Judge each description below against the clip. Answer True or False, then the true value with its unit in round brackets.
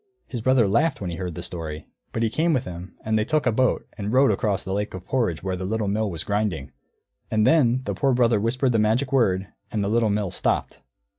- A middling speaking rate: False (245 wpm)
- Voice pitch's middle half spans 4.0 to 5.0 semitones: True (4.7 semitones)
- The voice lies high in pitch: False (110 Hz)